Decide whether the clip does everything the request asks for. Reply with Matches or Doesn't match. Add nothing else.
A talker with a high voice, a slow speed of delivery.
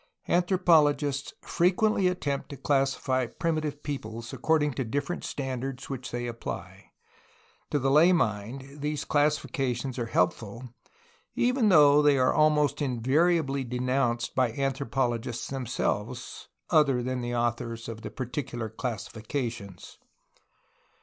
Doesn't match